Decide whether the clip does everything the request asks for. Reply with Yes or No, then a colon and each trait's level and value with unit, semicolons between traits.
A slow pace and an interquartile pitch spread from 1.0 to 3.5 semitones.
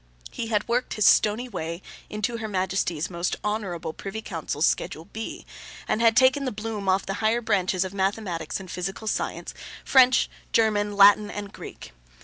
No: average, 165 wpm; average, 3.1 semitones